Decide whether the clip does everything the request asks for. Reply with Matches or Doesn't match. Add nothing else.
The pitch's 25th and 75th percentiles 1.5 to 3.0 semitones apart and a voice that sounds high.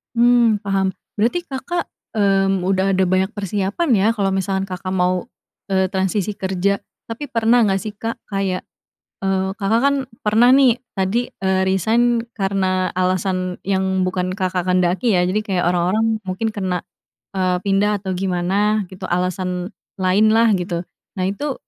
Matches